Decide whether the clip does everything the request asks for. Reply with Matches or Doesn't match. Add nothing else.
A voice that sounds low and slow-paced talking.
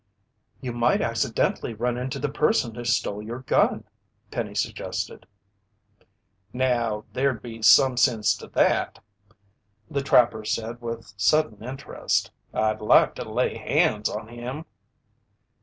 Matches